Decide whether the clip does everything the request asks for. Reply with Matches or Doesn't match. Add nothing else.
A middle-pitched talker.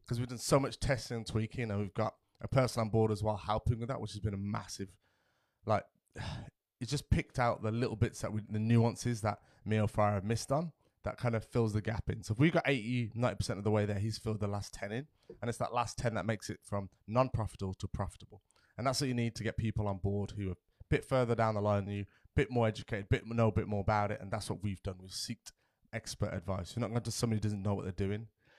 Doesn't match